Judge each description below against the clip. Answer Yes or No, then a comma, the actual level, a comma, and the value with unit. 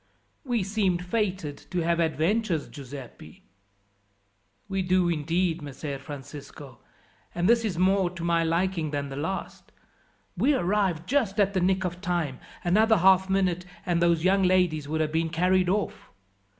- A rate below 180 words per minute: Yes, average, 150 wpm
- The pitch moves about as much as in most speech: Yes, average, 3.3 semitones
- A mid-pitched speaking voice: Yes, medium, 175 Hz